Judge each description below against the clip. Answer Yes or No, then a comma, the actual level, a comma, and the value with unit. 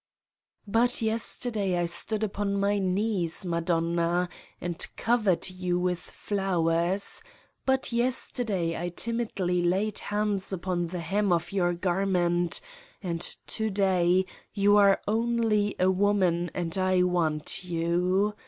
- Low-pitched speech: No, medium, 185 Hz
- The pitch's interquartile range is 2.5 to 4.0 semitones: Yes, average, 3.0 semitones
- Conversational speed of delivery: No, slow, 120 wpm